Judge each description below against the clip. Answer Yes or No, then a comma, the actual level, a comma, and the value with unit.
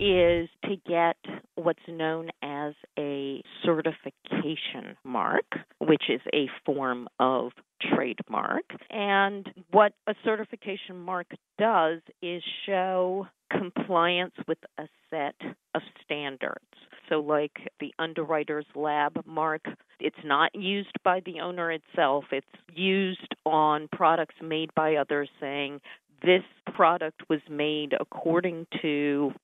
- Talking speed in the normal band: No, slow, 115 wpm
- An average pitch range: Yes, average, 3.7 semitones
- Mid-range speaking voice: Yes, medium, 165 Hz